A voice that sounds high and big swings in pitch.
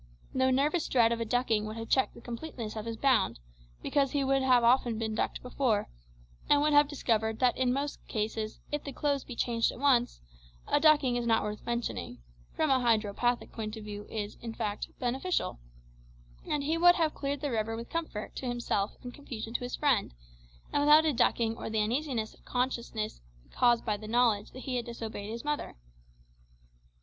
No: high, 240 Hz; average, 3.8 semitones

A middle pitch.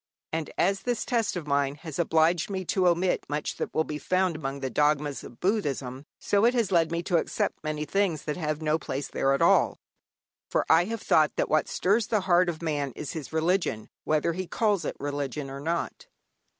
Yes: medium, 160 Hz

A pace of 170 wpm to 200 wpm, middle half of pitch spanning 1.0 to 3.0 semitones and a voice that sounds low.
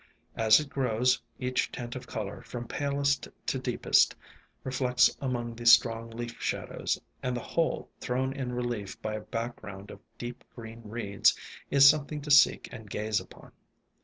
No: average, 160 wpm; narrow, 2.6 semitones; low, 120 Hz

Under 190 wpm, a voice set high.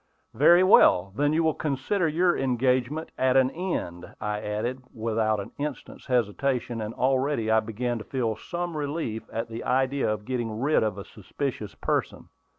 No: average, 165 wpm; low, 125 Hz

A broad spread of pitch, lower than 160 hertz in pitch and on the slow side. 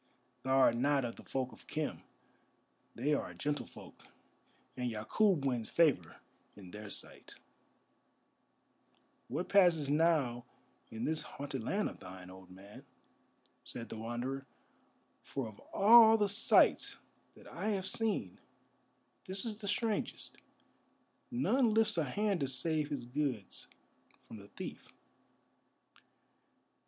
Yes: wide, 8.6 semitones; medium, 140 Hz; slow, 130 wpm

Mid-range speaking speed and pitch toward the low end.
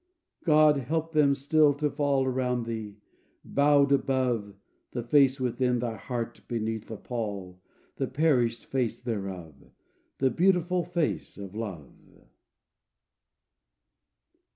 No: slow, 110 wpm; low, 125 Hz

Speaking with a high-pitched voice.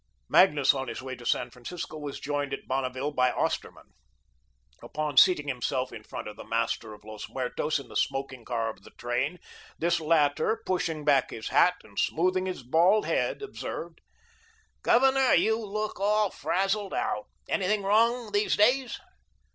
No: medium, 150 Hz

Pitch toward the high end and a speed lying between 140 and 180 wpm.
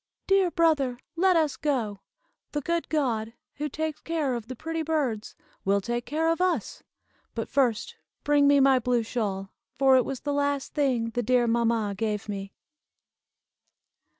Yes: very high, 265 Hz; average, 160 wpm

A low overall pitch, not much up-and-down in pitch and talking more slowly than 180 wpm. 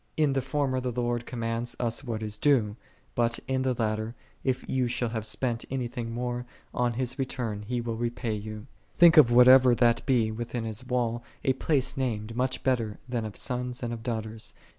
No: low, 120 Hz; narrow, 2.0 semitones; average, 195 wpm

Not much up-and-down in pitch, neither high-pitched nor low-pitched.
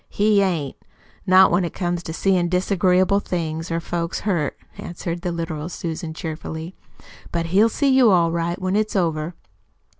Yes: narrow, 2.2 semitones; medium, 175 Hz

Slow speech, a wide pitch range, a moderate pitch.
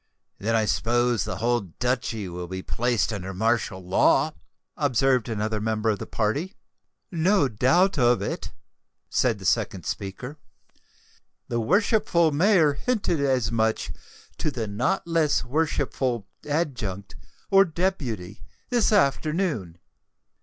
No: slow, 125 wpm; wide, 6.5 semitones; low, 125 Hz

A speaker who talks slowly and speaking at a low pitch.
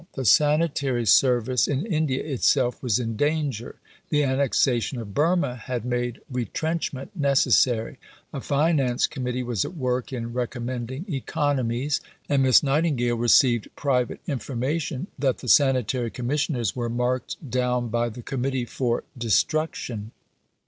Yes: slow, 130 wpm; low, 130 Hz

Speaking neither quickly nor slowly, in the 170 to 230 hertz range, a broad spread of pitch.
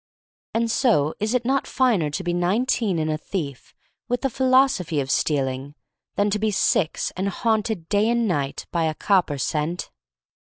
Yes: average, 180 wpm; high, 190 Hz; wide, 6.9 semitones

